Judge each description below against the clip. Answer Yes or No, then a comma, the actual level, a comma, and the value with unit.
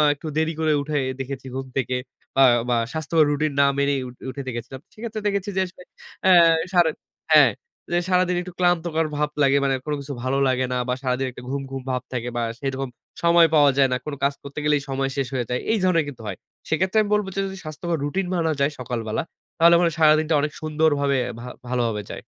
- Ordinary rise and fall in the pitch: Yes, average, 4.0 semitones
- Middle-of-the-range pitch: Yes, medium, 145 Hz